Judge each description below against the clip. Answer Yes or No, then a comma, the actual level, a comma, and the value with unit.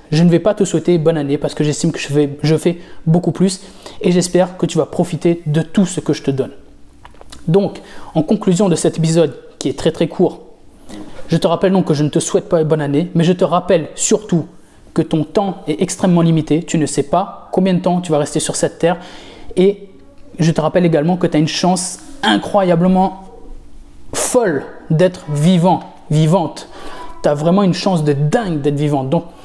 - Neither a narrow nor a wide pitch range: Yes, average, 3.1 semitones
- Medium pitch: Yes, medium, 165 Hz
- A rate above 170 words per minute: Yes, average, 210 wpm